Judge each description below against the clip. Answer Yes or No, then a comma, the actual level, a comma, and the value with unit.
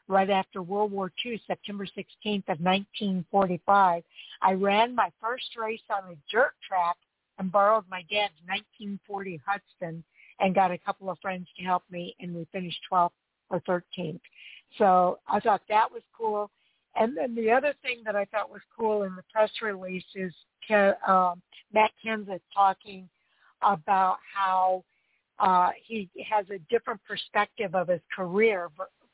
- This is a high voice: Yes, high, 195 Hz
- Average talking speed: Yes, average, 150 wpm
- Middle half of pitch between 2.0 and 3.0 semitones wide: Yes, narrow, 2.5 semitones